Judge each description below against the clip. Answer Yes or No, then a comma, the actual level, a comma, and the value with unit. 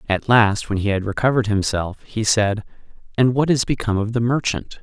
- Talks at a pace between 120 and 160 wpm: No, average, 200 wpm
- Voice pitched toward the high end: No, low, 110 Hz